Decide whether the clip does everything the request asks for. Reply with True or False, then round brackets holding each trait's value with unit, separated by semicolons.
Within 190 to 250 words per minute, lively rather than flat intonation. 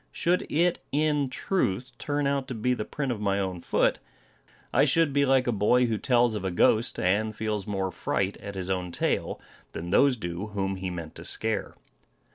True (200 wpm; 5.7 semitones)